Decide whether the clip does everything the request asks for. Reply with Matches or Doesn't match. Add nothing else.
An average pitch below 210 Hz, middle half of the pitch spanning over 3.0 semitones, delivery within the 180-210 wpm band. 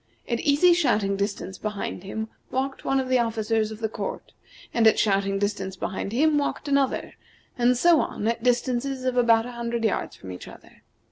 Doesn't match